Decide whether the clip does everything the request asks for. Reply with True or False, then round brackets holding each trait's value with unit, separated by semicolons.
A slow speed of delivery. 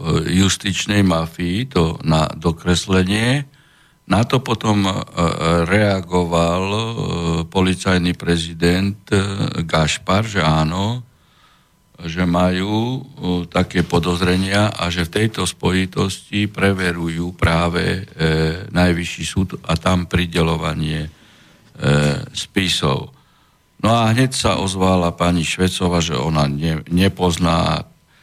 True (85 wpm)